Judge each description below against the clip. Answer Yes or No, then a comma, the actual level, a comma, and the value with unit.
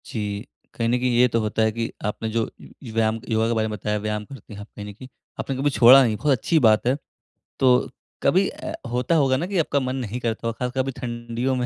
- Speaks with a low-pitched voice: Yes, low, 120 Hz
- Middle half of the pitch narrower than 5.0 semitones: Yes, average, 2.9 semitones